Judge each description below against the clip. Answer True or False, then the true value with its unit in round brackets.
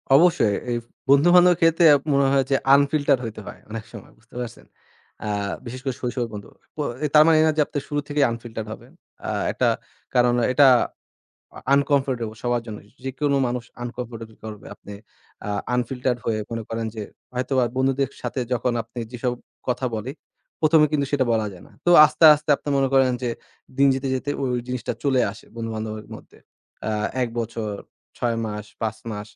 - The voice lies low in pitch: True (125 Hz)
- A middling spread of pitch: True (3.5 semitones)